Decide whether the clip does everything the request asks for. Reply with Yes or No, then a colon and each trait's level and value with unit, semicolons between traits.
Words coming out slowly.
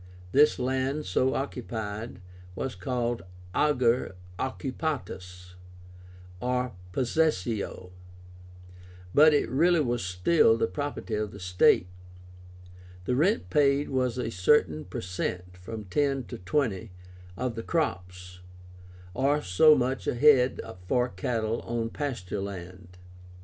Yes: slow, 115 wpm